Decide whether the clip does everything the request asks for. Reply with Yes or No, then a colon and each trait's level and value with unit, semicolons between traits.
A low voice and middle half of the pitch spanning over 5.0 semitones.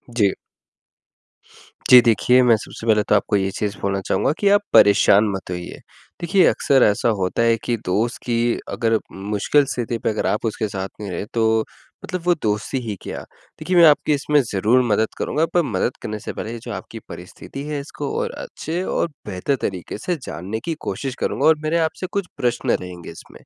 Yes: low, 115 Hz; wide, 5.6 semitones